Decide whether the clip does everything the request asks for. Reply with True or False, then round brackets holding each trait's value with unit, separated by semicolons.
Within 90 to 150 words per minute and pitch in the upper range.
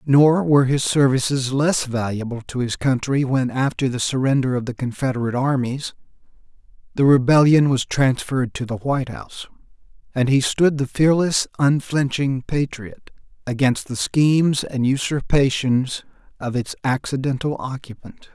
False (135 wpm; 135 Hz)